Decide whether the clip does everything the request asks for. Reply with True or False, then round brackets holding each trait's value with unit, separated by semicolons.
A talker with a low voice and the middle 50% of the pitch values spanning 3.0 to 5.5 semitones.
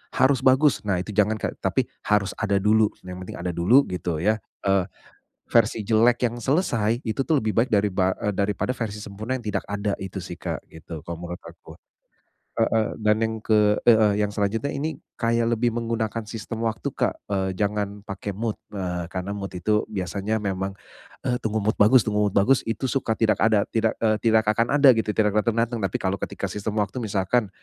False (105 Hz; 2.5 semitones)